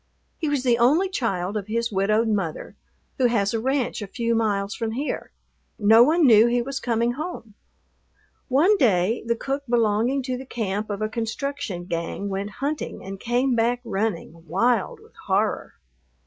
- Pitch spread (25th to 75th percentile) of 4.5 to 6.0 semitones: No, average, 4.0 semitones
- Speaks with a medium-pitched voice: No, high, 230 Hz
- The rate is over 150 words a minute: Yes, average, 170 wpm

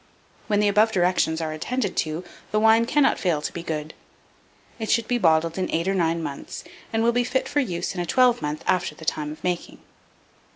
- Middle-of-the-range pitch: Yes, medium, 180 Hz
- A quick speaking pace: Yes, fast, 215 wpm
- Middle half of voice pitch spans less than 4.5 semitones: No, wide, 5.6 semitones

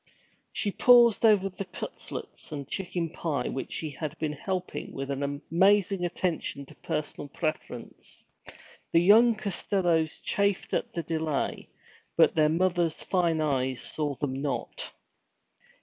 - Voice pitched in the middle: Yes, medium, 165 Hz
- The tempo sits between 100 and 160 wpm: Yes, slow, 135 wpm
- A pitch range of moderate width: Yes, average, 4.5 semitones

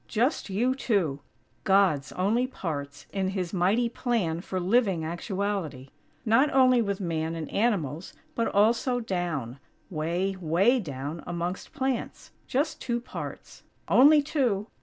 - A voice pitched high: Yes, high, 195 Hz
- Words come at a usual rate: No, slow, 130 wpm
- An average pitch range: No, wide, 6.1 semitones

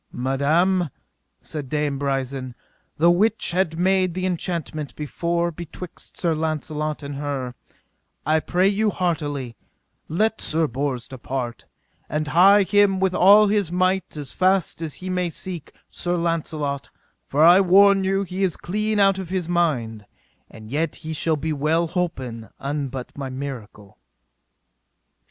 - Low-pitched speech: No, medium, 160 Hz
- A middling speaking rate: Yes, average, 145 wpm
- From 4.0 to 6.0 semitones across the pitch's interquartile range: Yes, average, 4.6 semitones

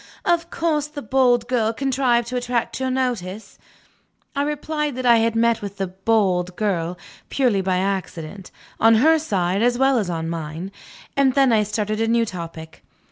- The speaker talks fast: No, average, 175 wpm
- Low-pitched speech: No, high, 225 Hz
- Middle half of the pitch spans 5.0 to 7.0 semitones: Yes, wide, 5.4 semitones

